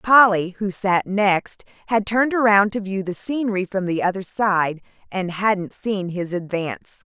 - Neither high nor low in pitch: No, high, 200 Hz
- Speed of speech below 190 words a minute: Yes, average, 170 wpm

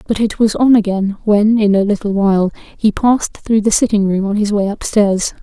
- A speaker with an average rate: No, fast, 220 wpm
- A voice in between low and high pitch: No, high, 210 Hz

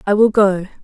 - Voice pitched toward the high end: Yes, high, 200 Hz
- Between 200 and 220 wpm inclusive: Yes, fast, 215 wpm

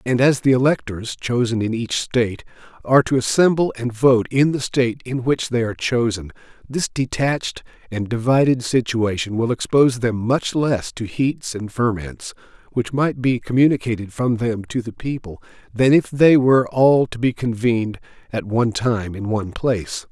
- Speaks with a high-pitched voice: No, low, 120 Hz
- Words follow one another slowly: No, average, 175 wpm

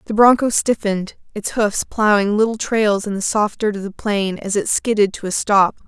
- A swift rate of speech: Yes, fast, 215 wpm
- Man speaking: No, female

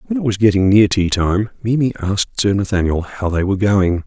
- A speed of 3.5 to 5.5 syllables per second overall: No, 5.7 syllables/s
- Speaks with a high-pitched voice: No, low, 100 Hz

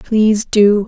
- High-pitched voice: Yes, high, 210 Hz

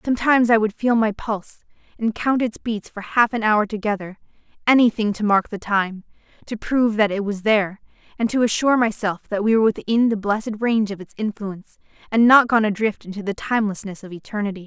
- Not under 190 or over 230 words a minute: Yes, average, 195 wpm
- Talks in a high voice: Yes, high, 215 Hz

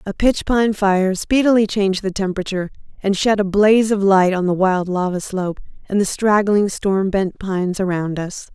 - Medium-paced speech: Yes, average, 190 wpm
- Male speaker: No, female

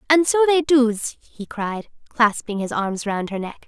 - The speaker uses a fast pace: No, average, 195 wpm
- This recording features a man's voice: No, female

